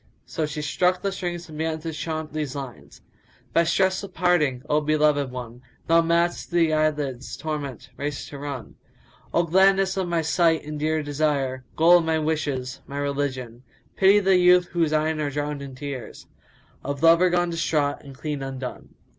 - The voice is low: No, medium, 155 Hz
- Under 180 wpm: No, average, 185 wpm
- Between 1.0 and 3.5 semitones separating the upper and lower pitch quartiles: Yes, average, 3.1 semitones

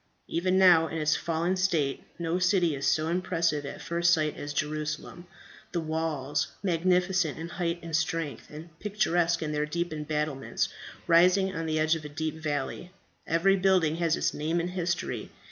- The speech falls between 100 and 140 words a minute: No, average, 170 wpm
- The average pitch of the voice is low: No, medium, 165 Hz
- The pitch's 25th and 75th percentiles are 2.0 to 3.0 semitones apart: Yes, narrow, 2.4 semitones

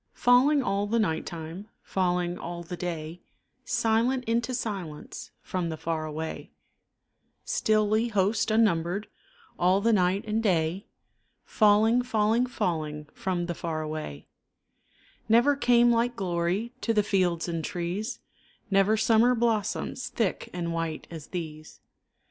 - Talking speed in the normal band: No, slow, 130 wpm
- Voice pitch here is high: Yes, high, 195 Hz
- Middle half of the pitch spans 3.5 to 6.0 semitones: Yes, average, 5.0 semitones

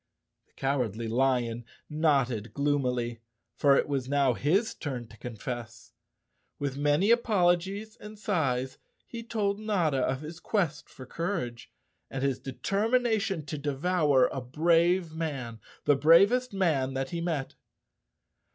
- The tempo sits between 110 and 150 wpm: Yes, slow, 135 wpm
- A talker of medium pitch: Yes, medium, 145 Hz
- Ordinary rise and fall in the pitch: No, wide, 5.8 semitones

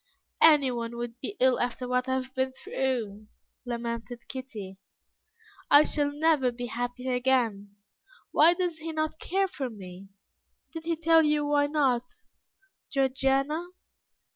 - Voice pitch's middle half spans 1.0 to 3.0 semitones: No, average, 3.8 semitones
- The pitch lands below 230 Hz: No, very high, 260 Hz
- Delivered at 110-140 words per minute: Yes, slow, 135 wpm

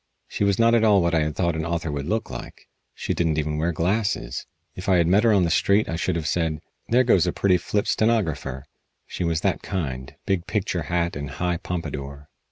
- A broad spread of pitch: No, average, 4.2 semitones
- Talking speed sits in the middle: No, fast, 225 wpm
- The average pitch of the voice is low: Yes, very low, 85 Hz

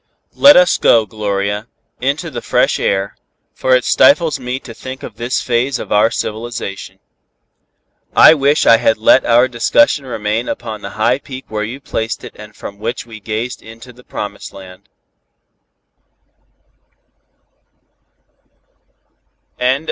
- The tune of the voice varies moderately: Yes, average, 3.3 semitones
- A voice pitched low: Yes, low, 115 Hz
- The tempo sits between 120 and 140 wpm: Yes, slow, 135 wpm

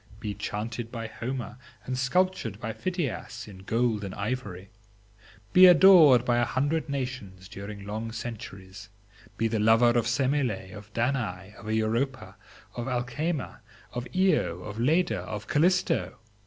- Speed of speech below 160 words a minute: Yes, average, 140 wpm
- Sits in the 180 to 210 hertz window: No, low, 115 Hz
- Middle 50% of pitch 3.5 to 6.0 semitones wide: Yes, average, 4.0 semitones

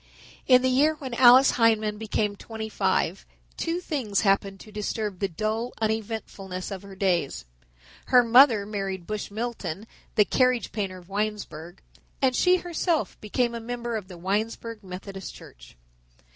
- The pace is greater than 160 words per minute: No, average, 150 wpm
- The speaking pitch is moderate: No, high, 215 Hz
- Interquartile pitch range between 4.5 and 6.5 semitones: No, average, 3.7 semitones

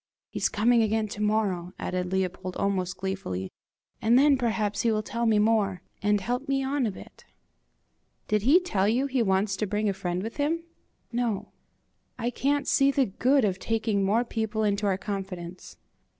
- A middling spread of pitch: Yes, average, 3.8 semitones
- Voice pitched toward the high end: Yes, high, 215 Hz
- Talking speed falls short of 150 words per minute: No, average, 180 wpm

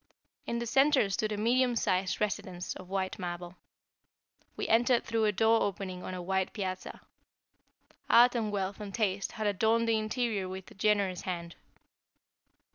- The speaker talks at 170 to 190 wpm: No, average, 160 wpm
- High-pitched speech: Yes, high, 205 Hz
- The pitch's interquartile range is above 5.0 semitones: No, average, 3.3 semitones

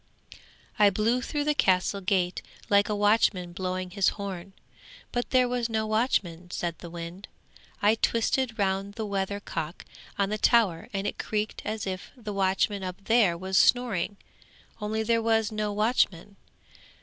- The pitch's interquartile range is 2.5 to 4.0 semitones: Yes, average, 3.0 semitones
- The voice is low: No, high, 205 Hz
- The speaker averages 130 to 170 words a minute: Yes, average, 160 wpm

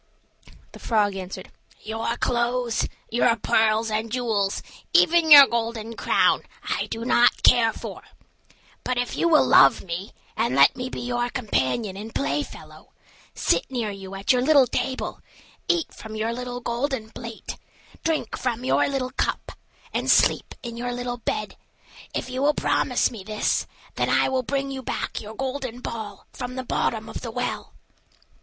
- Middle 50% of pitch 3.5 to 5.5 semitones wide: No, average, 2.8 semitones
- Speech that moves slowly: No, average, 165 wpm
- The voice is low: No, high, 240 Hz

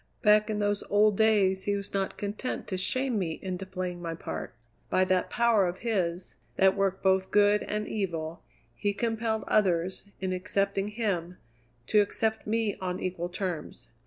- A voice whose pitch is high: Yes, high, 195 Hz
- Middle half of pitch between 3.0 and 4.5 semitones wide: No, narrow, 2.4 semitones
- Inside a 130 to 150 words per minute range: No, average, 165 wpm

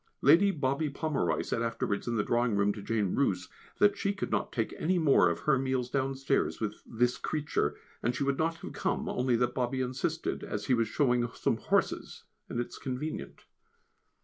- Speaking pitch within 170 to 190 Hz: No, low, 130 Hz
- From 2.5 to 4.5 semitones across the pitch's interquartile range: Yes, average, 3.7 semitones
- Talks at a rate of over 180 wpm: Yes, average, 195 wpm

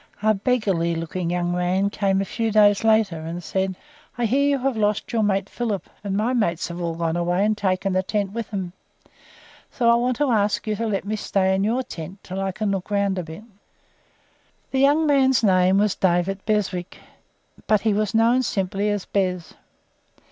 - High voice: Yes, high, 200 Hz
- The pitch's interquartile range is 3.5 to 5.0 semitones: No, average, 3.1 semitones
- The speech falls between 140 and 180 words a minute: No, average, 200 wpm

